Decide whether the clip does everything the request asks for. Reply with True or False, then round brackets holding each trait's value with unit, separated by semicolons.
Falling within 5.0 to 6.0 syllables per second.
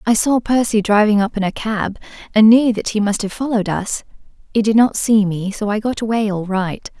True (5.3 syllables/s)